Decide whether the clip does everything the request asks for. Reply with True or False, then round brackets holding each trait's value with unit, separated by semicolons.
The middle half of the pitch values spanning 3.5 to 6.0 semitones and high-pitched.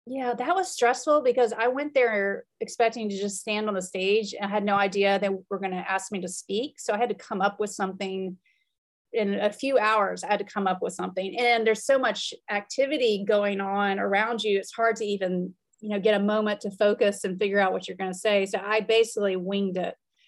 False (2.7 semitones; 210 Hz)